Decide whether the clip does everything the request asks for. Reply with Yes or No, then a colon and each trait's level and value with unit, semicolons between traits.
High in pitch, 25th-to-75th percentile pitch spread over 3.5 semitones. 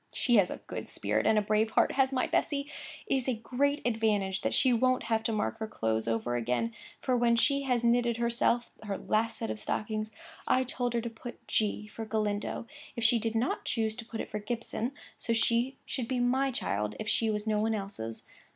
No: high, 225 Hz; narrow, 2.4 semitones